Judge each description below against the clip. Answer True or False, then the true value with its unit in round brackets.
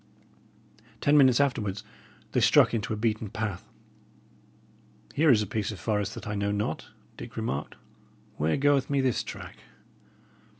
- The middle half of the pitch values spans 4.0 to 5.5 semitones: True (4.3 semitones)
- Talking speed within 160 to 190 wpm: False (145 wpm)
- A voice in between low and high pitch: False (110 Hz)